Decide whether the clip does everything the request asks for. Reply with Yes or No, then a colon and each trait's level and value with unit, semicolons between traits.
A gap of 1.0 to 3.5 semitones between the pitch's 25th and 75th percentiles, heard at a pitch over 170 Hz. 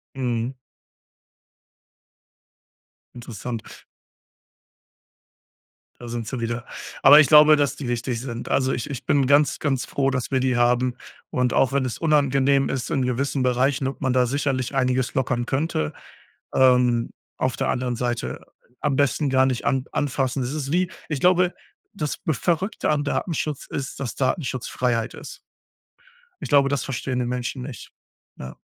No: narrow, 2.4 semitones; low, 130 Hz